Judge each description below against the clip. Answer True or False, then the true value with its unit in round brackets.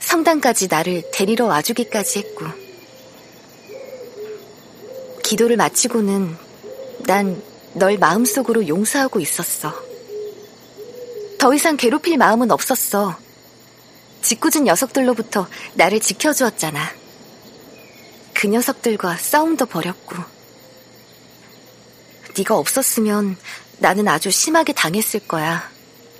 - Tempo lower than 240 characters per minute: True (220 characters per minute)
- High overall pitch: True (235 Hz)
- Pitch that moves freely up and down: True (7.5 semitones)